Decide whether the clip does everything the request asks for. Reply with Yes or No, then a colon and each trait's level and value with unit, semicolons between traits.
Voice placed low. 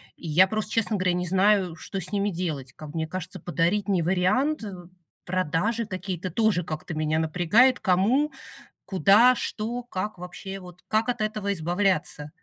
No: medium, 185 Hz